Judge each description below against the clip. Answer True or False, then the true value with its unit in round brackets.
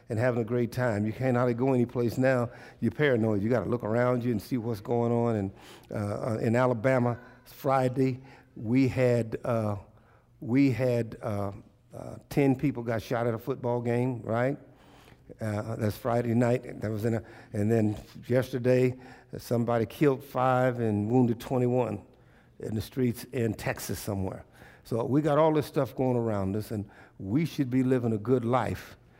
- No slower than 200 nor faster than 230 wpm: False (175 wpm)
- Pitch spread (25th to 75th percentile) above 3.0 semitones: False (2.4 semitones)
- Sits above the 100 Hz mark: True (120 Hz)